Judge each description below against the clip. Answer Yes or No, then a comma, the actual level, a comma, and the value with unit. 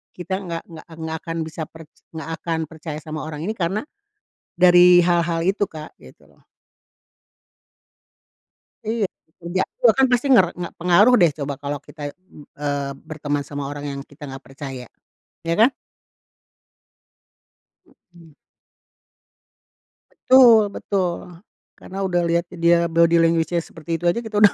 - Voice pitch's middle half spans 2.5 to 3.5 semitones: Yes, average, 3.0 semitones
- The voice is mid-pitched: Yes, medium, 170 Hz